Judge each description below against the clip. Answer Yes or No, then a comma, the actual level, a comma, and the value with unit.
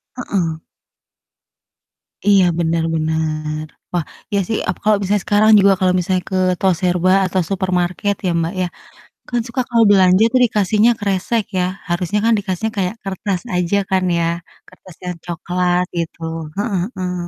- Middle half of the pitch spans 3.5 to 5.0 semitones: No, narrow, 2.6 semitones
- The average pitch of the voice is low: No, medium, 185 Hz